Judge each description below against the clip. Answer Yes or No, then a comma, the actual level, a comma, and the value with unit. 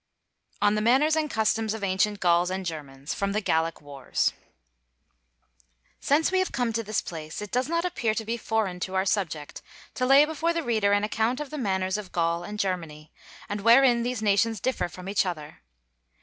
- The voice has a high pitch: Yes, high, 210 Hz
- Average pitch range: Yes, average, 4.9 semitones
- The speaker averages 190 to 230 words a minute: Yes, average, 195 wpm